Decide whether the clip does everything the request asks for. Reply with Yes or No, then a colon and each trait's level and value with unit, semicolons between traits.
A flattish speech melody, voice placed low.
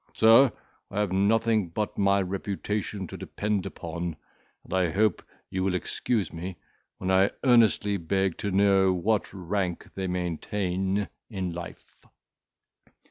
Yes: narrow, 2.3 semitones; very low, 95 Hz